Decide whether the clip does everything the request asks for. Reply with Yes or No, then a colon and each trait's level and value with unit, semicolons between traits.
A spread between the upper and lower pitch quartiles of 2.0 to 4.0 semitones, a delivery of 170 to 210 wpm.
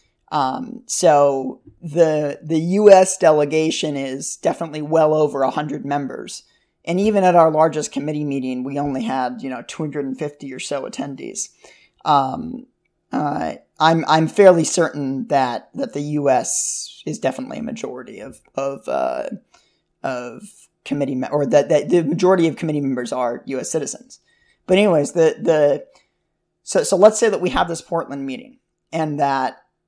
No: average, 3.5 semitones; average, 155 wpm